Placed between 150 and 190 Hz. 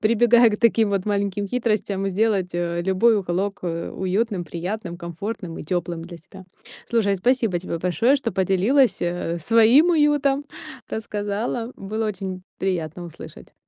No: high, 200 Hz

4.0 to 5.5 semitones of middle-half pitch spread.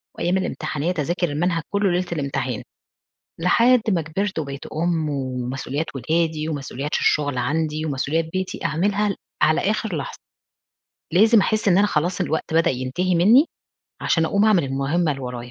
Yes: average, 4.5 semitones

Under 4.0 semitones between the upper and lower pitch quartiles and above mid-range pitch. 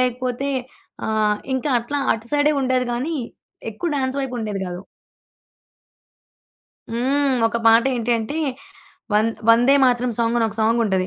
Yes: average, 2.9 semitones; high, 240 Hz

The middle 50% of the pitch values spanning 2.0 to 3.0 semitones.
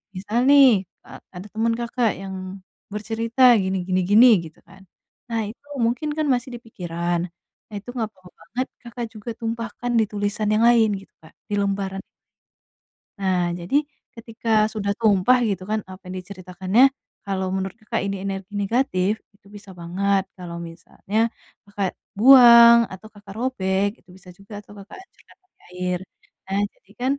No: average, 3.5 semitones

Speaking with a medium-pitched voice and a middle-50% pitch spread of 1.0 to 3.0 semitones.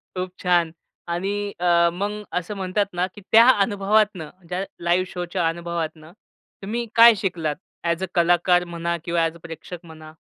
Yes: medium, 180 Hz; average, 2.7 semitones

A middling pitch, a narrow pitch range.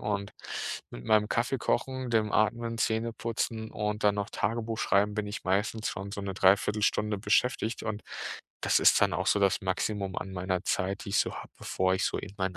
No: low, 105 Hz; narrow, 2.3 semitones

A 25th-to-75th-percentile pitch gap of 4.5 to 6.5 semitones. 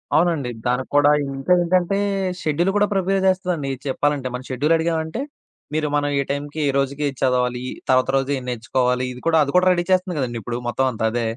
Yes: average, 4.9 semitones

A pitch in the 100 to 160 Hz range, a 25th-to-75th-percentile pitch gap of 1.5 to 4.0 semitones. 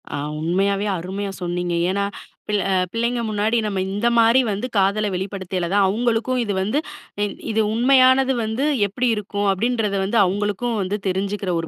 No: high, 205 Hz; average, 3.1 semitones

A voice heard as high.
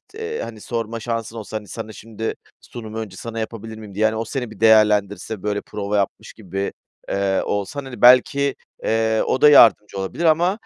No: low, 110 Hz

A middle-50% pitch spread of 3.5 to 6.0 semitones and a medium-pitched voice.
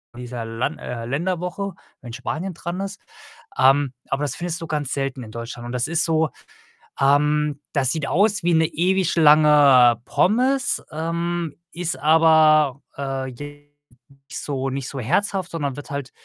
Yes: average, 4.1 semitones; medium, 150 Hz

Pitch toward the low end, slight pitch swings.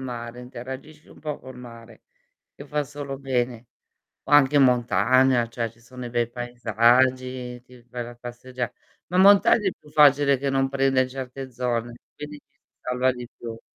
Yes: low, 125 Hz; narrow, 2.0 semitones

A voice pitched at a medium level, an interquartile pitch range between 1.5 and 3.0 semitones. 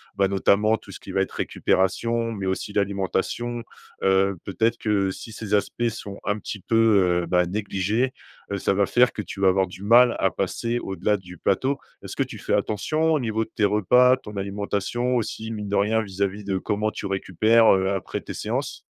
No: low, 105 Hz; average, 2.7 semitones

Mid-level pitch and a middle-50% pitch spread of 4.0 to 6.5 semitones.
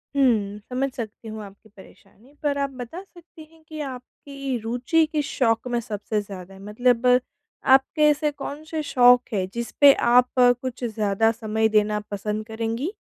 No: high, 240 Hz; average, 4.4 semitones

